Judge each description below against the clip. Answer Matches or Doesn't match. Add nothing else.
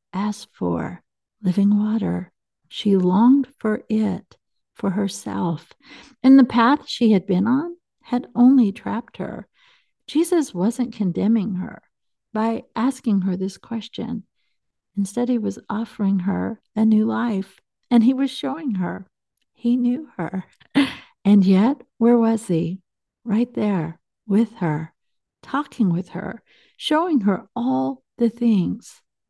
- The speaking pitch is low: Doesn't match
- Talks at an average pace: Doesn't match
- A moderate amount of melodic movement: Matches